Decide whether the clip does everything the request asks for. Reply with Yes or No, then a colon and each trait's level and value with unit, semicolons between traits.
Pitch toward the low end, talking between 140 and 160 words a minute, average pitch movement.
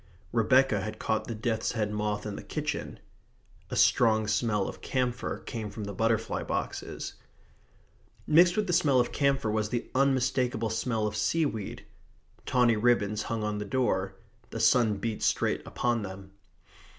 Yes: low, 110 Hz; average, 155 wpm; average, 3.0 semitones